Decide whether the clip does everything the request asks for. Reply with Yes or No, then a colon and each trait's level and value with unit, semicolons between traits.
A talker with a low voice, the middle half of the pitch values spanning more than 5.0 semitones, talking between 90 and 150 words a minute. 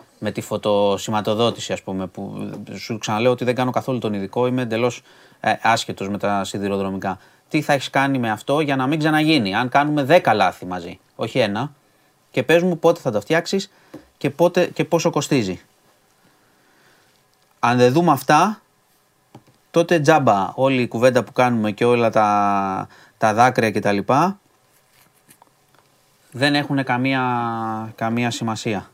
Yes: low, 125 Hz; wide, 5.4 semitones; average, 145 wpm